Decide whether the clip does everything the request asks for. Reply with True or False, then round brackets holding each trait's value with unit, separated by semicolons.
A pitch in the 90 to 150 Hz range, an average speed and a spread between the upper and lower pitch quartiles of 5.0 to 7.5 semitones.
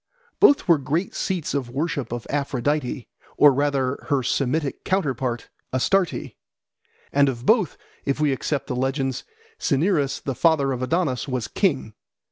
False (140 Hz; 150 wpm; 3.5 semitones)